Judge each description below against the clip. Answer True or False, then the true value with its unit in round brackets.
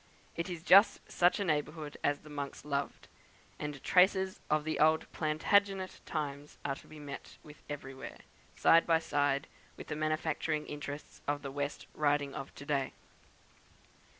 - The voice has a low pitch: False (150 Hz)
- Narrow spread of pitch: True (1.9 semitones)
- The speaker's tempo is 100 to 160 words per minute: True (155 wpm)